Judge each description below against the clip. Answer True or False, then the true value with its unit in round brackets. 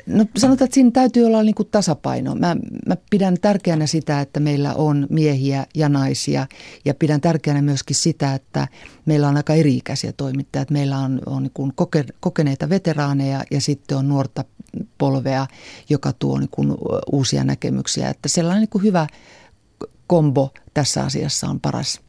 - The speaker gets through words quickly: True (165 wpm)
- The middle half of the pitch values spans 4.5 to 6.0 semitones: False (3.7 semitones)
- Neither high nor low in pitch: True (145 Hz)